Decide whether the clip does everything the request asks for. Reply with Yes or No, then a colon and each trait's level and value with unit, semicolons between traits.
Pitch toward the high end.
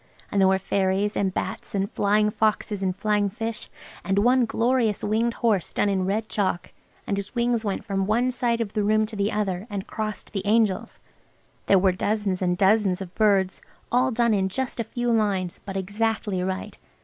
Yes: high, 205 Hz